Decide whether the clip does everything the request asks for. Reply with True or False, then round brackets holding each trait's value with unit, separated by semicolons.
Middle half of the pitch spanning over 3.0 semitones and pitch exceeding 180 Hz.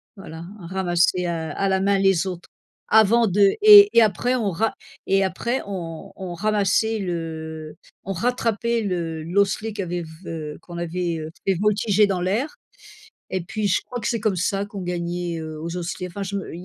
True (3.5 semitones; 190 Hz)